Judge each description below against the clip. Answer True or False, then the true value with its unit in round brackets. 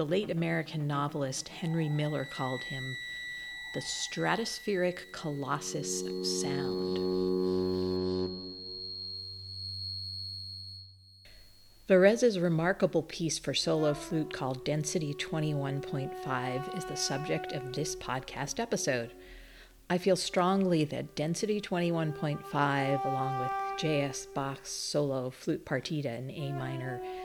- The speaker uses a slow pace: True (100 wpm)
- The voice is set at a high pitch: False (140 Hz)